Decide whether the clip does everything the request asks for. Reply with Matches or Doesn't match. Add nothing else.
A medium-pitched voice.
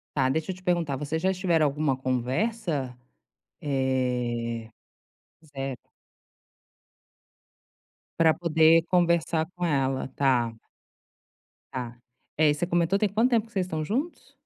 Matches